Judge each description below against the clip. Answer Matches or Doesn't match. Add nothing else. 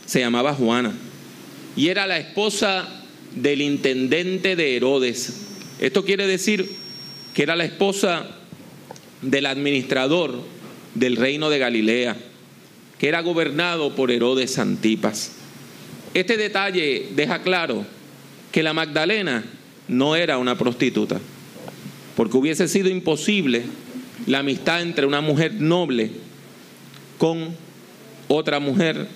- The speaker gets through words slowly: Matches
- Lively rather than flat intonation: Matches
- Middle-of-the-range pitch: Matches